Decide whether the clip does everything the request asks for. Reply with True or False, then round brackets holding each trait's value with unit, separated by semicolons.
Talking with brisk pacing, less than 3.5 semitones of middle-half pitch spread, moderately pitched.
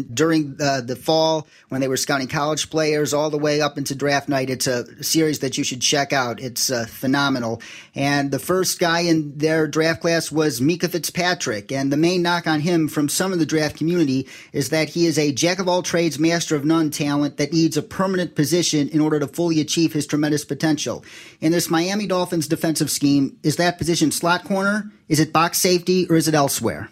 True (215 wpm; 2.9 semitones; 155 Hz)